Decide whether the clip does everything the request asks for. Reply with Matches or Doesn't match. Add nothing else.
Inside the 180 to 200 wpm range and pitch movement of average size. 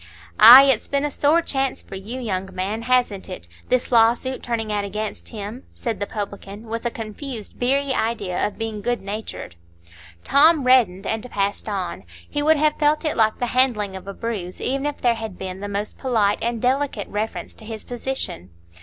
Matches